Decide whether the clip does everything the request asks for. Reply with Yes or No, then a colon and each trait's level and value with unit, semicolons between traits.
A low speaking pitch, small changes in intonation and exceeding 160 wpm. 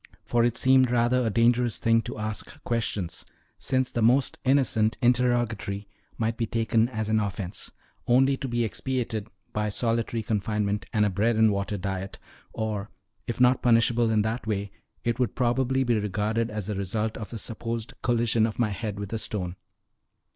Yes: low, 115 Hz; narrow, 2.2 semitones; average, 175 wpm